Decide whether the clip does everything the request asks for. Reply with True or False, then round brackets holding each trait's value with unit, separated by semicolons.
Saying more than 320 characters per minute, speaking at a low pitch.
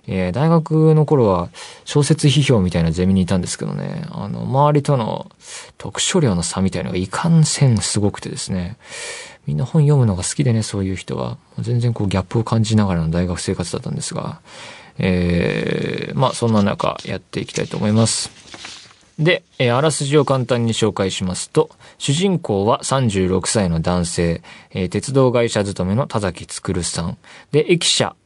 True (335 characters per minute; 110 Hz)